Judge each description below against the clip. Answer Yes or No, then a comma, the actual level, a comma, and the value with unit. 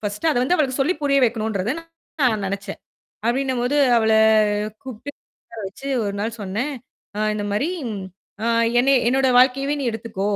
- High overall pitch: Yes, high, 240 Hz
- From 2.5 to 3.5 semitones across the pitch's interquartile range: No, average, 4.3 semitones